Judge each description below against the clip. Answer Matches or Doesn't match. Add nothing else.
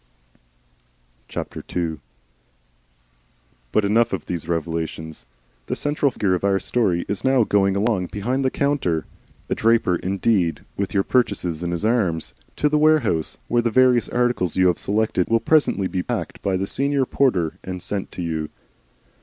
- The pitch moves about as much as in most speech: Doesn't match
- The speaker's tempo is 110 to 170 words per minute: Matches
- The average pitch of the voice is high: Doesn't match